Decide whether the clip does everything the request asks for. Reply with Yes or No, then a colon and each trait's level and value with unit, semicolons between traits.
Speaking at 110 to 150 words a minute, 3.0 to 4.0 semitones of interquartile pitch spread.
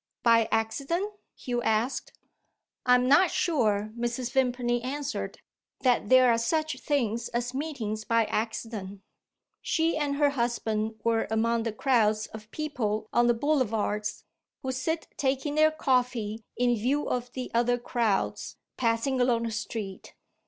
Yes: average, 140 wpm; average, 3.3 semitones